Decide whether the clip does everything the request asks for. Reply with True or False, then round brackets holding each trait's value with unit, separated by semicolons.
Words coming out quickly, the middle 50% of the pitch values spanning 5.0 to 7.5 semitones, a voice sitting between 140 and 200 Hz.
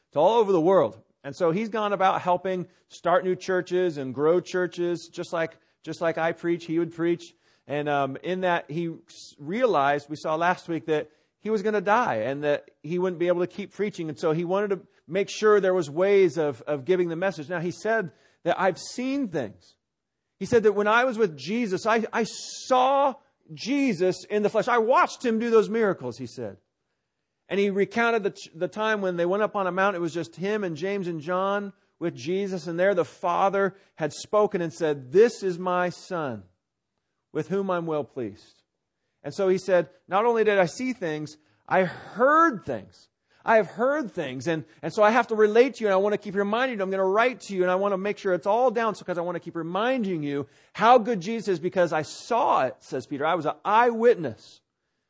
False (225 wpm; 4.0 semitones; 185 Hz)